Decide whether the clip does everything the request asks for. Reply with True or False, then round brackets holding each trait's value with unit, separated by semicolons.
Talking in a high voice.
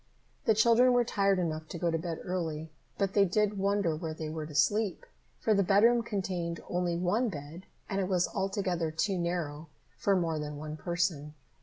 False (180 Hz)